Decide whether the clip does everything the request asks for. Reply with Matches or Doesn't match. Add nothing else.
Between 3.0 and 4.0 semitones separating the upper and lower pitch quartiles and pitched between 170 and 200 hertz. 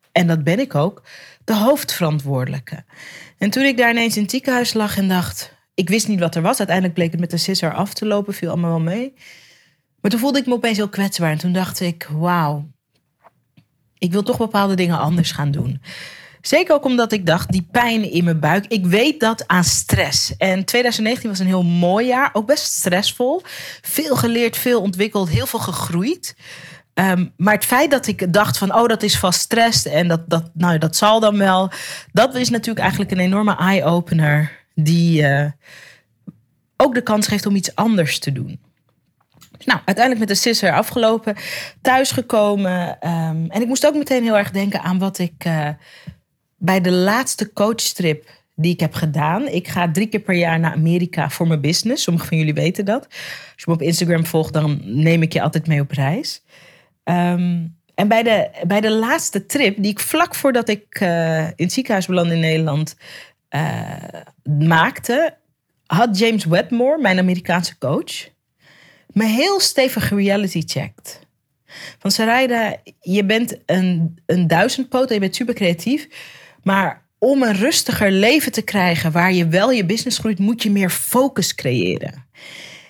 Doesn't match